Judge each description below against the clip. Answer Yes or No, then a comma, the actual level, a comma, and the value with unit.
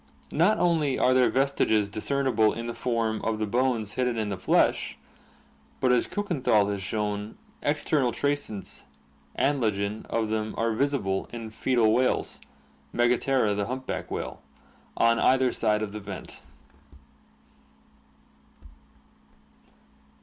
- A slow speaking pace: Yes, slow, 120 wpm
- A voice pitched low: Yes, low, 115 Hz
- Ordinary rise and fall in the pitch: Yes, average, 3.5 semitones